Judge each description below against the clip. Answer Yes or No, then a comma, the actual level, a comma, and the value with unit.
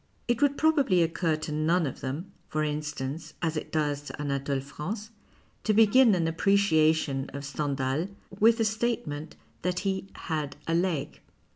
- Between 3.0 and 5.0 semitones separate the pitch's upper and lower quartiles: No, wide, 5.4 semitones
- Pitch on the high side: No, medium, 160 Hz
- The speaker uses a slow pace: No, average, 160 wpm